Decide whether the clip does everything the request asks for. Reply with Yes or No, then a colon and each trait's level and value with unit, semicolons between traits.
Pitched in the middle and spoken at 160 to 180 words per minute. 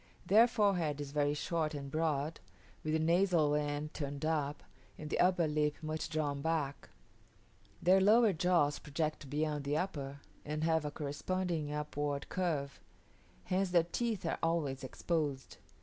No: medium, 155 Hz; average, 150 wpm